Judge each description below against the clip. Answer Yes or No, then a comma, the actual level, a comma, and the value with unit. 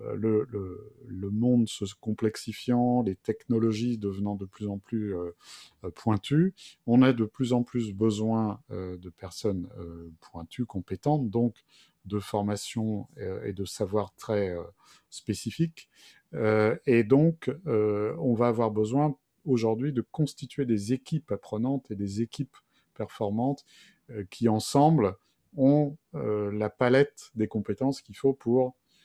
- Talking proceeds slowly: Yes, slow, 140 wpm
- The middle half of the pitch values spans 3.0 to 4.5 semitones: Yes, average, 3.9 semitones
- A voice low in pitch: Yes, low, 110 Hz